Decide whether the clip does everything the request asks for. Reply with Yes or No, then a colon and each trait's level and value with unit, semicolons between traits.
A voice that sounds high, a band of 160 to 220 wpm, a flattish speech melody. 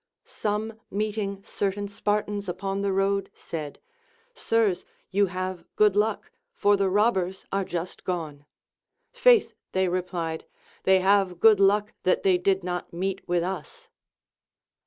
No: high, 195 Hz; slow, 135 wpm; narrow, 2.2 semitones